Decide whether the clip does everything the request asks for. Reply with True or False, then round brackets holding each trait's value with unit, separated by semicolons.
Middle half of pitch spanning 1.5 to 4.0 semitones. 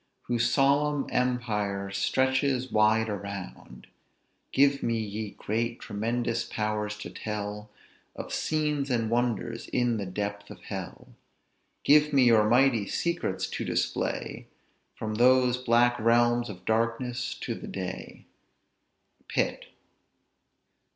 True (3.1 semitones)